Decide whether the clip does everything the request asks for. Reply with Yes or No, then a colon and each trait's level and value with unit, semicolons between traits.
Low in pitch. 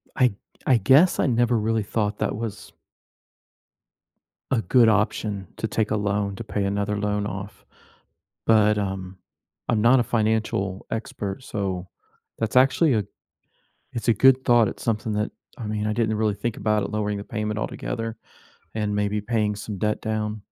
Yes: low, 105 Hz